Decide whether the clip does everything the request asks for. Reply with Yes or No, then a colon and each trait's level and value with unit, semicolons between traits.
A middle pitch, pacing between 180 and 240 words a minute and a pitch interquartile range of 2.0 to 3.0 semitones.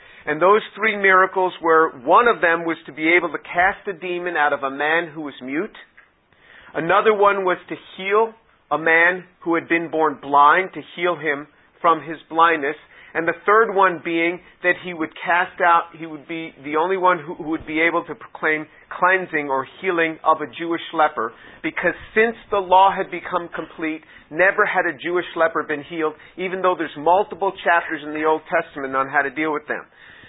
Yes: medium, 170 Hz; average, 200 wpm; narrow, 2.6 semitones